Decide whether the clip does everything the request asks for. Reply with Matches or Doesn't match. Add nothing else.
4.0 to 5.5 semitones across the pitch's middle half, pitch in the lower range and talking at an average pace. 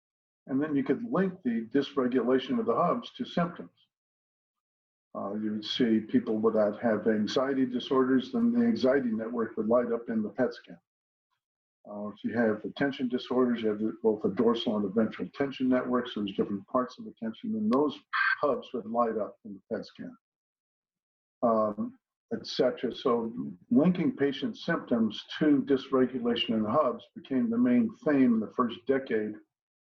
Matches